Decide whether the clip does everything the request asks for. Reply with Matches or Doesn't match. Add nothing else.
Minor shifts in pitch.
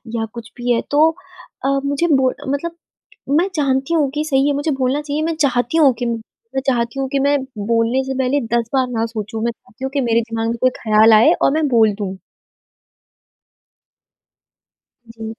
Doesn't match